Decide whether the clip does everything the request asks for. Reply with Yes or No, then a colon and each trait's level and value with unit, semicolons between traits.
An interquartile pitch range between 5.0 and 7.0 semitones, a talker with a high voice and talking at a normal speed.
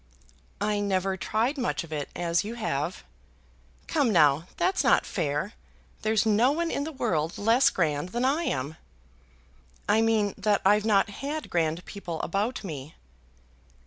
Yes: wide, 5.4 semitones; high, 200 Hz; average, 150 wpm